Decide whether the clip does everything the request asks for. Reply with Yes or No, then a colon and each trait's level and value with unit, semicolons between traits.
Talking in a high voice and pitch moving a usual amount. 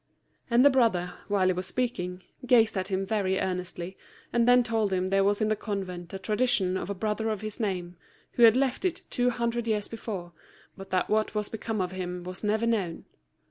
Yes: high, 205 Hz; average, 3.6 semitones